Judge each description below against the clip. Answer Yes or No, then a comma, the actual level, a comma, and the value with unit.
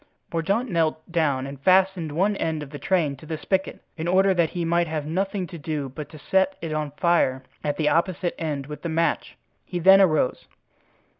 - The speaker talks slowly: No, fast, 205 wpm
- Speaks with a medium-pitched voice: Yes, medium, 165 Hz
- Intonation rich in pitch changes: No, average, 3.5 semitones